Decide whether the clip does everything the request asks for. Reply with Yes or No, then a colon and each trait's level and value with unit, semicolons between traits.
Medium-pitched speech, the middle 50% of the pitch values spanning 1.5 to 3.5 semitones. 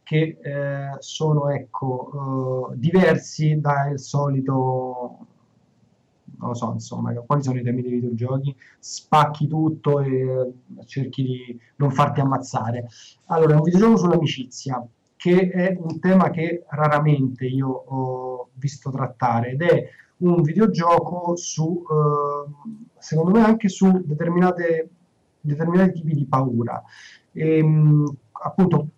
No: medium, 145 Hz; average, 4.0 semitones